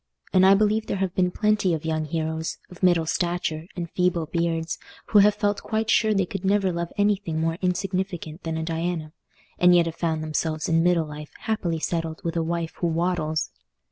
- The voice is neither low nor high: Yes, medium, 170 Hz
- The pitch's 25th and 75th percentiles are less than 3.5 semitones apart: Yes, average, 2.8 semitones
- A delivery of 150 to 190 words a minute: No, average, 200 wpm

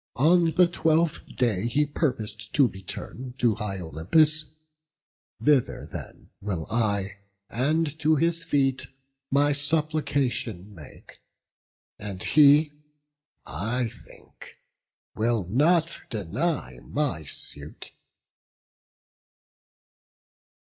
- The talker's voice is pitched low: Yes, low, 130 Hz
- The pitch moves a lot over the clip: Yes, wide, 6.9 semitones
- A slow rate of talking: Yes, slow, 90 wpm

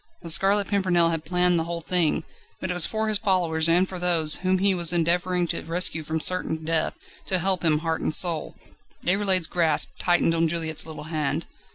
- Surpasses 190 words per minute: Yes, average, 200 wpm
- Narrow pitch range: Yes, narrow, 2.3 semitones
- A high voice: No, medium, 170 Hz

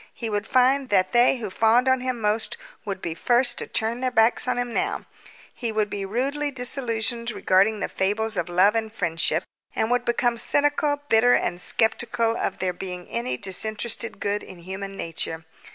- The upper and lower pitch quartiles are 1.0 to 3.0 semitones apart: No, average, 4.0 semitones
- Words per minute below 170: No, average, 185 wpm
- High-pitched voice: Yes, high, 225 Hz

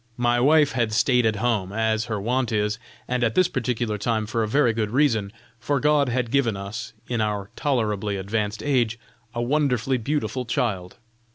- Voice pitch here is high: No, low, 115 Hz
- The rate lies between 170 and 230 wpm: Yes, average, 180 wpm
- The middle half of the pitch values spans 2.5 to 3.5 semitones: Yes, average, 2.9 semitones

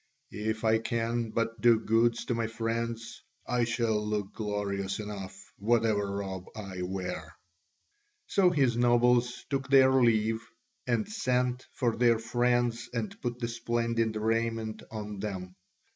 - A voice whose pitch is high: No, low, 115 Hz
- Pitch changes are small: Yes, narrow, 2.1 semitones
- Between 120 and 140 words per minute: Yes, slow, 135 wpm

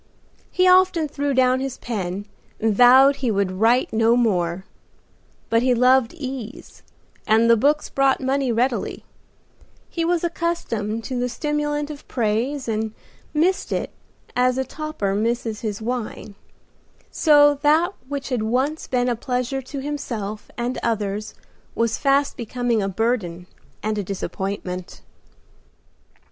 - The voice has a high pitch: Yes, high, 245 Hz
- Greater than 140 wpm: No, slow, 135 wpm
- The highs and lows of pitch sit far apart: No, average, 4.4 semitones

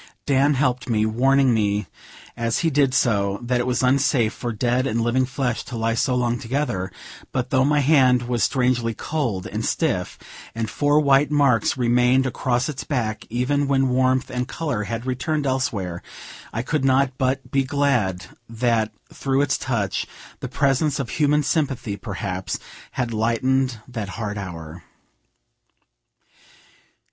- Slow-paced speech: No, average, 155 wpm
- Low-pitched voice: Yes, low, 125 Hz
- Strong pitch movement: No, average, 3.1 semitones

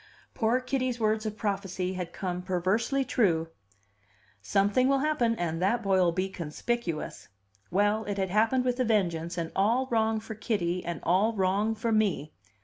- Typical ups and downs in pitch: Yes, average, 4.1 semitones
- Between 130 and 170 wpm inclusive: Yes, average, 160 wpm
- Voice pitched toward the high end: Yes, high, 205 Hz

